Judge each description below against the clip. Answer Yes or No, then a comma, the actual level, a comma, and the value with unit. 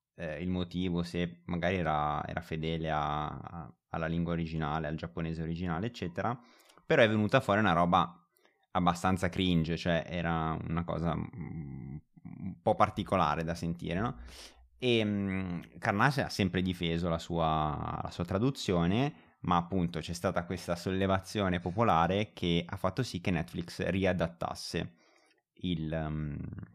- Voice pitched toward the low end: Yes, very low, 85 Hz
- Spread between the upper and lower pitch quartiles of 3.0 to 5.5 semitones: No, narrow, 2.5 semitones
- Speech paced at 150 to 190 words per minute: No, average, 135 wpm